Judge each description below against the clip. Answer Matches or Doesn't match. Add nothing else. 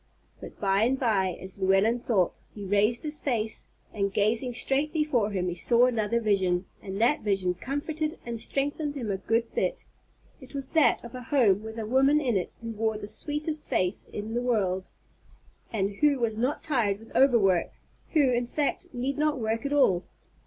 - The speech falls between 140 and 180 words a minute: Doesn't match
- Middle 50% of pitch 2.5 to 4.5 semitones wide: Doesn't match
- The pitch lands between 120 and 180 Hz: Doesn't match